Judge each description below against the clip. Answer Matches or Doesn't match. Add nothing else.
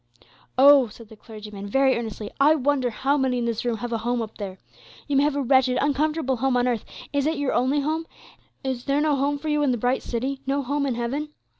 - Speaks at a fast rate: Matches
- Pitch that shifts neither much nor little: Matches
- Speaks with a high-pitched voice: Matches